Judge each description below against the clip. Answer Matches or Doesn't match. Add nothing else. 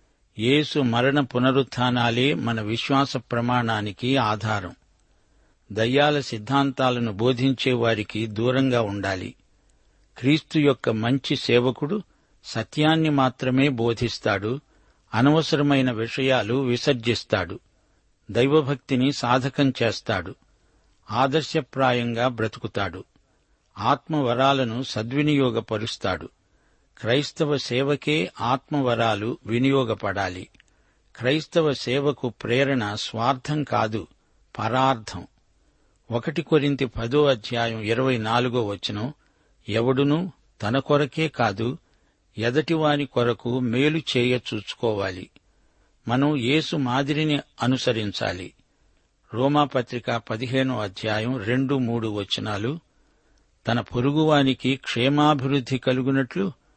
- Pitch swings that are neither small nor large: Matches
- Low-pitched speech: Matches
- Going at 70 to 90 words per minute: Matches